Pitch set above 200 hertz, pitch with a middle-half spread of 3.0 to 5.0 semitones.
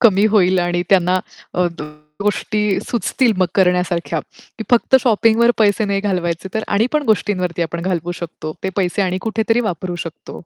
No: high, 190 Hz; average, 3.6 semitones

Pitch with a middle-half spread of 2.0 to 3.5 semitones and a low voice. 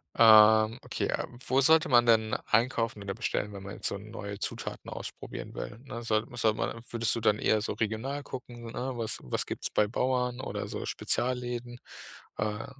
Yes: narrow, 2.4 semitones; low, 115 Hz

